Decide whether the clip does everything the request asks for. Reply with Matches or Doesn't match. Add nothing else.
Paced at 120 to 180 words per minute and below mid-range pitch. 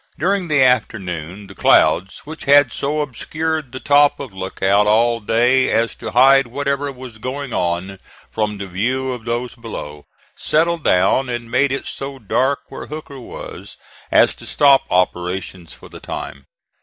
Matches